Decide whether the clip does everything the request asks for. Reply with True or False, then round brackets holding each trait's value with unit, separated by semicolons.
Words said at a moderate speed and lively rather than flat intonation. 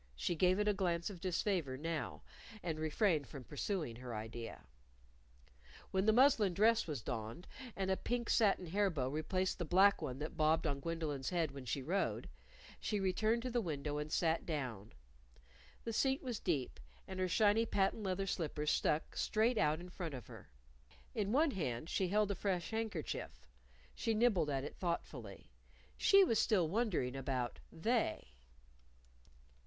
True (165 wpm; 6.0 semitones)